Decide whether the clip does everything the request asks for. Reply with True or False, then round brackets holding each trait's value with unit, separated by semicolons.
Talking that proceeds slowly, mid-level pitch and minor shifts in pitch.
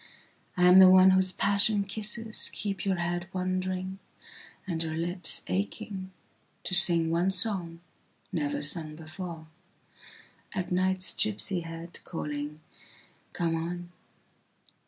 True (95 wpm; 180 Hz; 2.2 semitones)